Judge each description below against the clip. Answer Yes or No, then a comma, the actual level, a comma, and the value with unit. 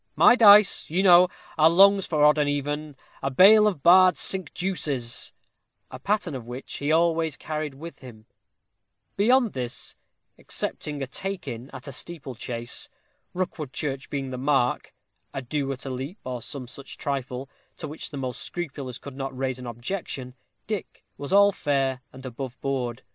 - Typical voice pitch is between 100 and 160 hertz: Yes, medium, 140 Hz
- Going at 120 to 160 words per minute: No, average, 170 wpm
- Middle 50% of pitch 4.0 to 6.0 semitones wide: Yes, average, 5.0 semitones